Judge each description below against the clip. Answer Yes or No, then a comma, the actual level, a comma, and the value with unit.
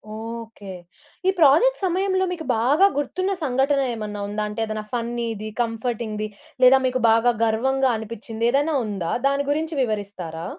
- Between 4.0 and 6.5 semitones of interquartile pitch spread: Yes, average, 4.7 semitones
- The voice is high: Yes, high, 235 Hz